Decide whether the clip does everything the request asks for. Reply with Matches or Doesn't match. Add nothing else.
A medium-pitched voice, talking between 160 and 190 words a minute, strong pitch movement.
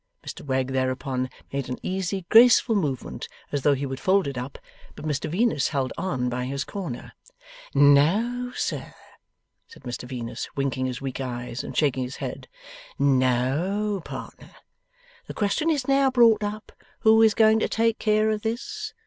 Matches